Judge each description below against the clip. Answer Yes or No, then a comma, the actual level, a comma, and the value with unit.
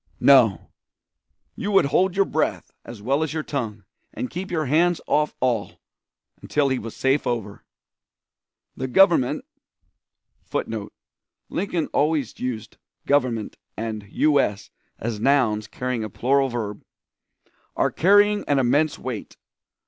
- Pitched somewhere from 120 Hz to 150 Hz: Yes, low, 135 Hz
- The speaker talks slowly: Yes, slow, 130 wpm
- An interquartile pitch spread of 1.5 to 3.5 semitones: No, average, 5.3 semitones